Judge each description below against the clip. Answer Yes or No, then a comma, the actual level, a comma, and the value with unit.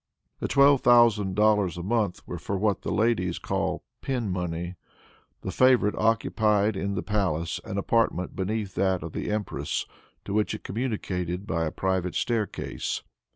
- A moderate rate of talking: Yes, average, 160 wpm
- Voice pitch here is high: No, low, 100 Hz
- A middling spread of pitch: Yes, average, 3.2 semitones